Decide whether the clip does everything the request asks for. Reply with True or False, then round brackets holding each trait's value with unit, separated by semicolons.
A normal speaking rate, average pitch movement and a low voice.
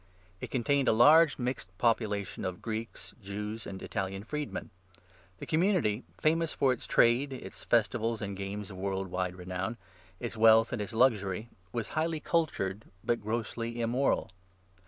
True (155 wpm; 4.5 semitones; 115 Hz)